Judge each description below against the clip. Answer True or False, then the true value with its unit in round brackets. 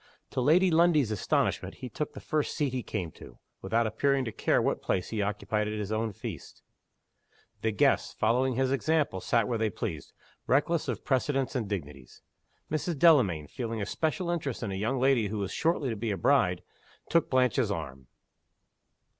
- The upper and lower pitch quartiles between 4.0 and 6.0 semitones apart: True (5.2 semitones)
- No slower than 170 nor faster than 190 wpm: True (180 wpm)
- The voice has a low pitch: True (120 Hz)